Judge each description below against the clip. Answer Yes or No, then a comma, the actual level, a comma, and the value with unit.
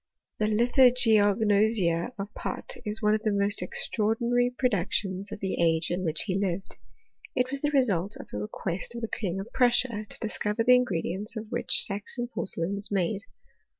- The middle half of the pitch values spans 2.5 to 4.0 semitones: Yes, average, 3.6 semitones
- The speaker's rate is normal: Yes, average, 180 wpm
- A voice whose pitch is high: Yes, high, 210 Hz